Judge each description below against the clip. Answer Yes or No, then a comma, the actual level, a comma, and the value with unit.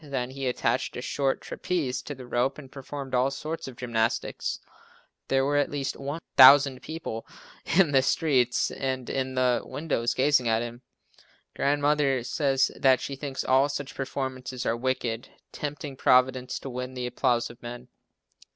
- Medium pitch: No, low, 130 Hz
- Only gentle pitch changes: Yes, narrow, 2.0 semitones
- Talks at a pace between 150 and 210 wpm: Yes, average, 160 wpm